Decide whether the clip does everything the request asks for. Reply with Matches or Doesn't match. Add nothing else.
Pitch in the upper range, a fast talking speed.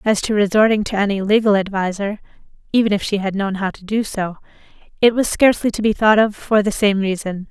Matches